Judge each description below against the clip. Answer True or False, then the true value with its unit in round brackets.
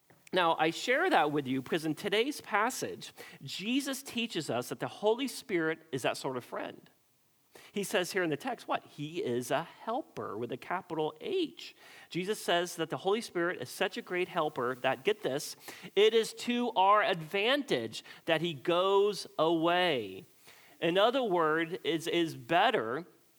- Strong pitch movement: True (6.1 semitones)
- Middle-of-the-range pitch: True (180 Hz)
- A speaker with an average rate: True (165 wpm)